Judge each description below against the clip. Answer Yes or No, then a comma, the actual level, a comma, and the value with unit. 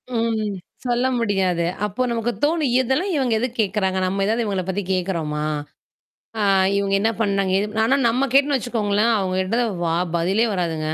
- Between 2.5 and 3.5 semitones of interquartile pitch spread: No, average, 4.1 semitones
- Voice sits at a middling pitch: No, high, 210 Hz